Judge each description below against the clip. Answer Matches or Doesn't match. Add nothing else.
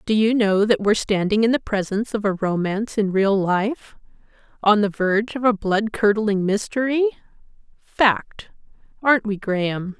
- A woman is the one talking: Matches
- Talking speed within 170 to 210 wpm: Doesn't match